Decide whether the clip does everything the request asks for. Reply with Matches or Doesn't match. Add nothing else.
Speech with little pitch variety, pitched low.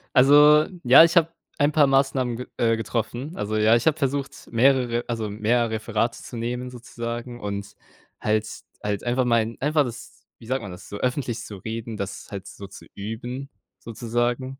Doesn't match